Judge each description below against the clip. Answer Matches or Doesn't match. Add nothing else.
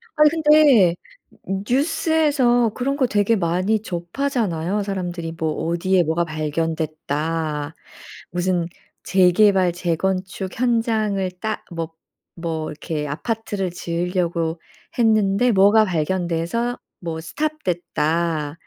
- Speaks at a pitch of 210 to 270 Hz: Doesn't match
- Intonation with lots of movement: Doesn't match